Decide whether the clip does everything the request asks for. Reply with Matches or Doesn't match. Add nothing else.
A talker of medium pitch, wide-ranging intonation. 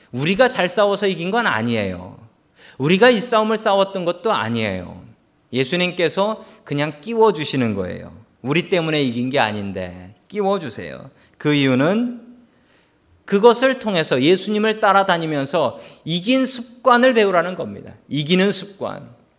Matches